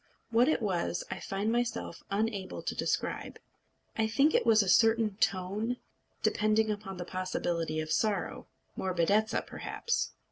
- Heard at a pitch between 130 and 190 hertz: No, high, 210 Hz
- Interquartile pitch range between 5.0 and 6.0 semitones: No, average, 3.3 semitones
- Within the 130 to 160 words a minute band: Yes, average, 140 wpm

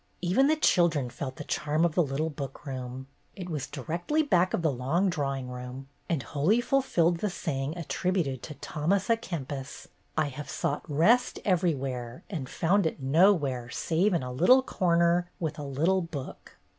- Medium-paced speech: Yes, average, 170 wpm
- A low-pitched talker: No, medium, 160 Hz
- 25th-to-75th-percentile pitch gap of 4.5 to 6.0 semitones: Yes, average, 4.8 semitones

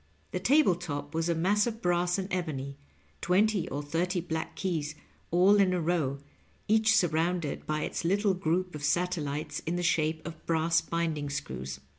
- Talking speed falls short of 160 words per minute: No, average, 175 wpm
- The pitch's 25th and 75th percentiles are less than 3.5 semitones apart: Yes, average, 2.9 semitones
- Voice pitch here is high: No, medium, 170 Hz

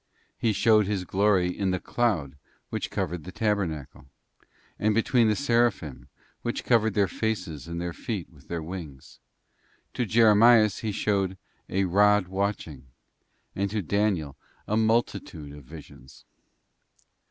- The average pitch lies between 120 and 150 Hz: No, low, 100 Hz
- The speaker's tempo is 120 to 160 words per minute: Yes, slow, 135 wpm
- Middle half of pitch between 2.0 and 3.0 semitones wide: No, average, 4.3 semitones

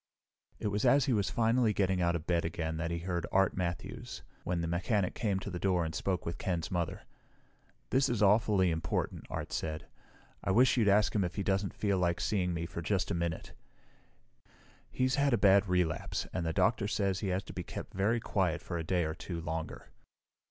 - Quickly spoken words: Yes, fast, 210 wpm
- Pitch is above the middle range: No, very low, 95 Hz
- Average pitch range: Yes, average, 3.3 semitones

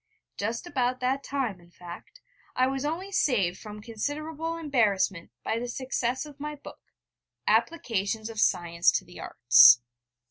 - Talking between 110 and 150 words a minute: Yes, average, 145 wpm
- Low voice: No, high, 245 Hz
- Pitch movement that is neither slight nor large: No, wide, 6.7 semitones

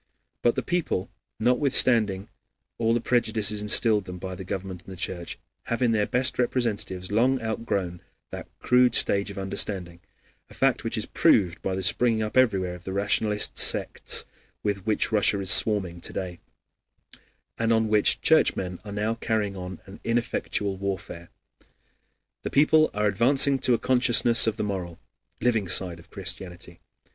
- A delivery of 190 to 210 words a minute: No, average, 165 wpm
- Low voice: Yes, low, 105 Hz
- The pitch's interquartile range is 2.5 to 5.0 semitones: Yes, average, 3.7 semitones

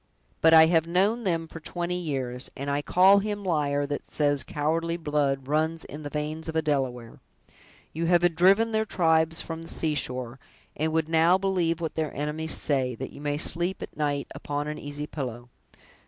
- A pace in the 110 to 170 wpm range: No, average, 185 wpm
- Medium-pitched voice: Yes, medium, 160 Hz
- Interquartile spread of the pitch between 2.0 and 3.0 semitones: Yes, narrow, 2.6 semitones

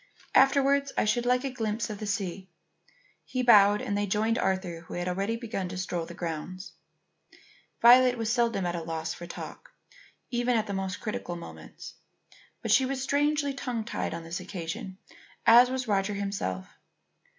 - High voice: Yes, high, 210 Hz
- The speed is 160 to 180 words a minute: Yes, average, 175 wpm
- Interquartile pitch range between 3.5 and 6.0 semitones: Yes, average, 5.1 semitones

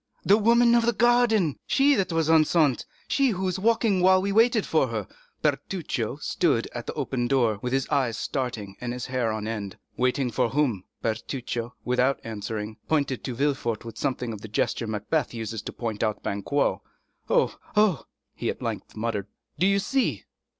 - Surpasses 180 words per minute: No, average, 170 wpm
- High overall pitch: No, low, 130 Hz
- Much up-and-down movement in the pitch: Yes, wide, 8.7 semitones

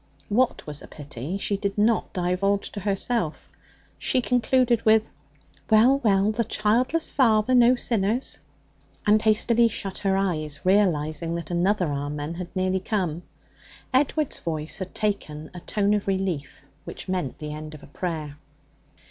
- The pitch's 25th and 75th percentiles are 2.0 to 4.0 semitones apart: No, average, 5.0 semitones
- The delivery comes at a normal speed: Yes, average, 150 wpm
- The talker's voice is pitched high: Yes, high, 195 Hz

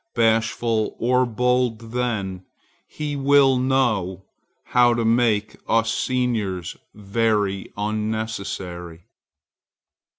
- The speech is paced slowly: Yes, slow, 80 wpm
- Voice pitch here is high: No, low, 115 Hz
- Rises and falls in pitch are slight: No, average, 3.3 semitones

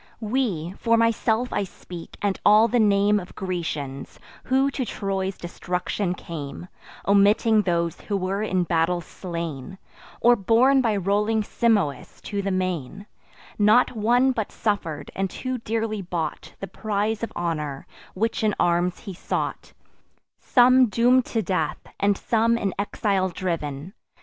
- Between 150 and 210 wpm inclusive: No, average, 140 wpm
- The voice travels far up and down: No, average, 4.2 semitones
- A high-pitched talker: Yes, high, 200 Hz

